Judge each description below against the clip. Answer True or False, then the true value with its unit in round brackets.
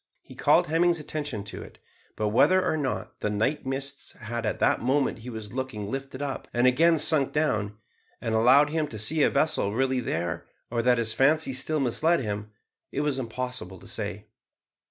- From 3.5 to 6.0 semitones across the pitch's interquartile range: True (4.8 semitones)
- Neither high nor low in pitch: False (130 Hz)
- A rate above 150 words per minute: True (190 wpm)